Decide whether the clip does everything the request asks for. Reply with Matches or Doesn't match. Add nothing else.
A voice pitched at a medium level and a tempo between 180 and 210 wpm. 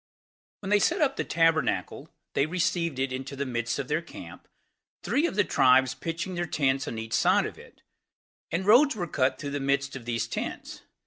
Matches